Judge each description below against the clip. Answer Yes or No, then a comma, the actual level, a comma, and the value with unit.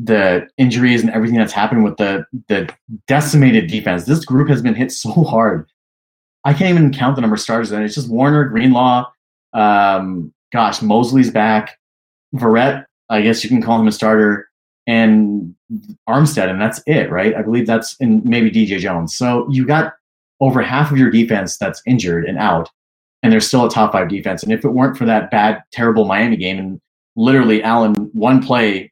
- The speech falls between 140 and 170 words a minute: No, average, 190 wpm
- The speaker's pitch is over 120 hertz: No, low, 115 Hz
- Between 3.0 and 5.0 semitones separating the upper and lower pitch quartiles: Yes, average, 3.5 semitones